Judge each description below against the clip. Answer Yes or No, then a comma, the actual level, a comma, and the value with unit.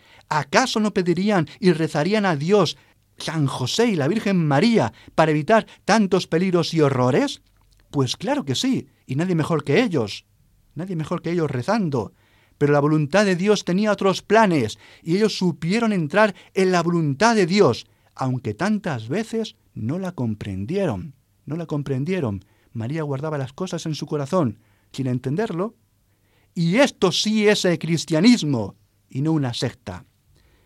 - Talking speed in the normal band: Yes, average, 155 wpm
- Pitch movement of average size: No, wide, 7.2 semitones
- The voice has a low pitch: No, medium, 160 Hz